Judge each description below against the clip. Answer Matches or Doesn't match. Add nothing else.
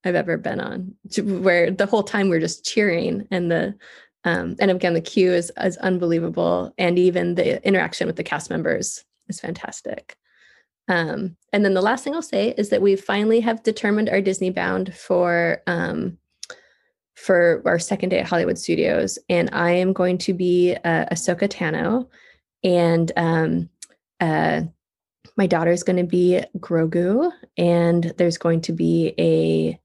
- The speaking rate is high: Doesn't match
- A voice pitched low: Doesn't match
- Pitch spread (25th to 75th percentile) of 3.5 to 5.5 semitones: Doesn't match